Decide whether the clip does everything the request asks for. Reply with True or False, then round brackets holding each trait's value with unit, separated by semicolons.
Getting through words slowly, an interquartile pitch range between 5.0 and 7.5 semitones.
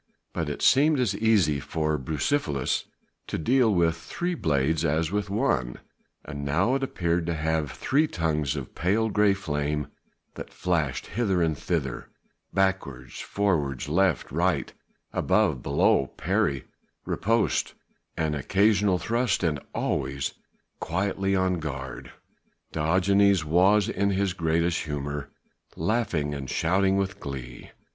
True (125 wpm; 5.3 semitones)